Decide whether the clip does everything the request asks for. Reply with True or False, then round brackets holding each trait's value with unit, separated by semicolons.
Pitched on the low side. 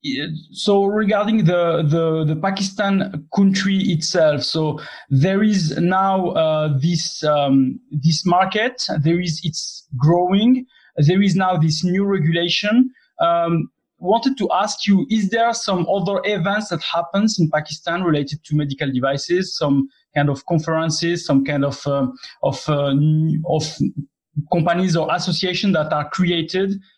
False (170 Hz)